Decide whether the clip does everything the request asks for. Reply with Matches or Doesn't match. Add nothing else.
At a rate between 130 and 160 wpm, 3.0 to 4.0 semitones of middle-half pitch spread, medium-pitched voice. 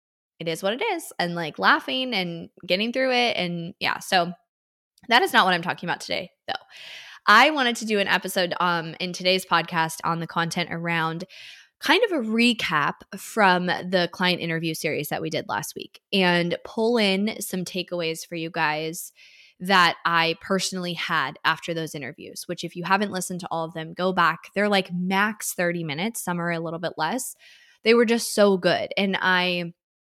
Doesn't match